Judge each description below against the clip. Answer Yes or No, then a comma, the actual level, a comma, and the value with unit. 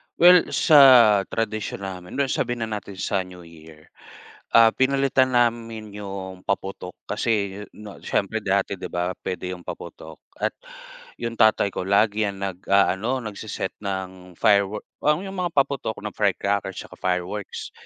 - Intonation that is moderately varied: Yes, average, 3.5 semitones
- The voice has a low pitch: Yes, low, 100 Hz